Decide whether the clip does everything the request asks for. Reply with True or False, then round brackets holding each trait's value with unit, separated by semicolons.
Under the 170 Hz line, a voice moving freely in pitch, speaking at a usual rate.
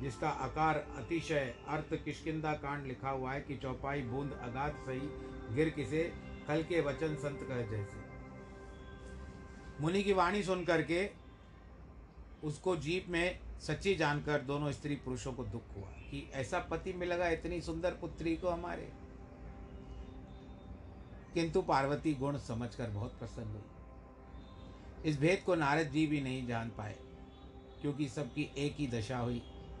True (140 Hz; 8.0 semitones; 140 wpm)